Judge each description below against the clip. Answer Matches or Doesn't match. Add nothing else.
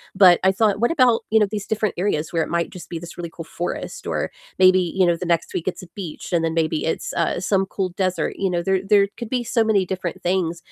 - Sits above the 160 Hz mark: Matches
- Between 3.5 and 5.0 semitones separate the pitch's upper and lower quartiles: Doesn't match